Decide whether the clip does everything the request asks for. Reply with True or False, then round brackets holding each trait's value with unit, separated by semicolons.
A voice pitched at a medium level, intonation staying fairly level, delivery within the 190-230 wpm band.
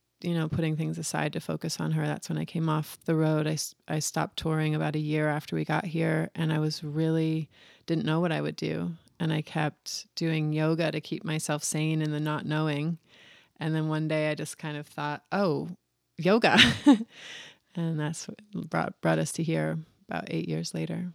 True (155 Hz; 1.6 semitones; 205 wpm)